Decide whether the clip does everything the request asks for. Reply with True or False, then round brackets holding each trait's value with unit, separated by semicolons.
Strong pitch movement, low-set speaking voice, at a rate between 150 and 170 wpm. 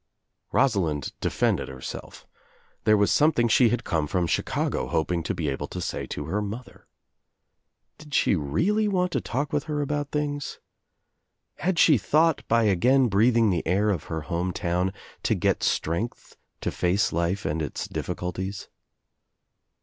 True (8.8 semitones; 105 Hz; 155 wpm)